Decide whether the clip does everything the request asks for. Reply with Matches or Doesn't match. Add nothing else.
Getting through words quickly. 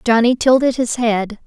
Doesn't match